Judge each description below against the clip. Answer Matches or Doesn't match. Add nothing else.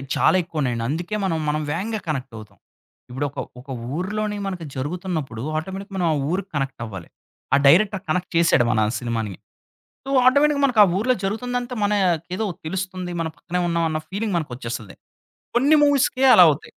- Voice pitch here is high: Doesn't match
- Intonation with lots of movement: Matches